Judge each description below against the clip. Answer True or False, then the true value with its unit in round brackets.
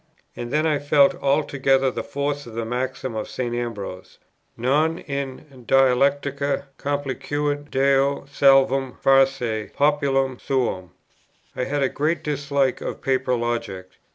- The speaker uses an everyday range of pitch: False (2.2 semitones)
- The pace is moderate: False (125 wpm)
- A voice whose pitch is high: False (135 Hz)